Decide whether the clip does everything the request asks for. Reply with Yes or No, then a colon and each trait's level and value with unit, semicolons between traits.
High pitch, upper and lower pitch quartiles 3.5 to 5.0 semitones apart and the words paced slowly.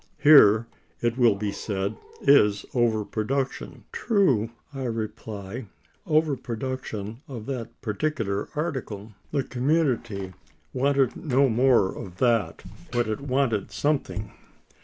No: low, 120 Hz; average, 4.3 semitones; slow, 115 wpm